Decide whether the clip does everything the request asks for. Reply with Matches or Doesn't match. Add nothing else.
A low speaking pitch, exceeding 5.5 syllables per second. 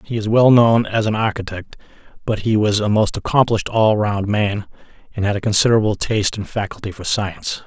Matches